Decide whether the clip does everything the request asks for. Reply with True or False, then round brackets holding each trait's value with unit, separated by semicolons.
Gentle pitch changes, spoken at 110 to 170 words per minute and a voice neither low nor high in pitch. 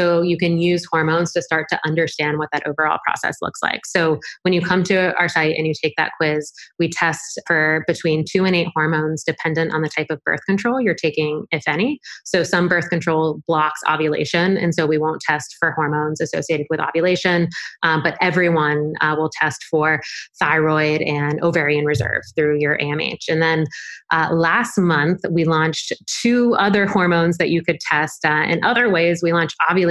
False (2.0 semitones; 195 wpm; 160 Hz)